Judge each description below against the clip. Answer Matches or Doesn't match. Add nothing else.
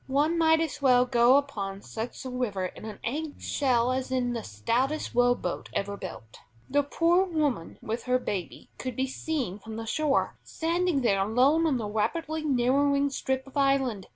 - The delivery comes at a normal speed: Matches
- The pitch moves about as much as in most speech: Matches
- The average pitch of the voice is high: Matches